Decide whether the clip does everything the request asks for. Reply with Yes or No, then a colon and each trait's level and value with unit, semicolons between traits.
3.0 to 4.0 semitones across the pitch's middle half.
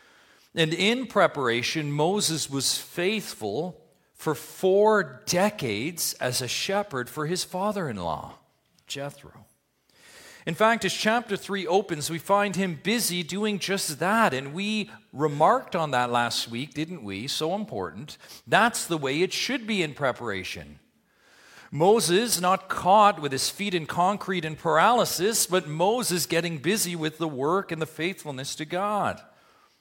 No: average, 5.1 semitones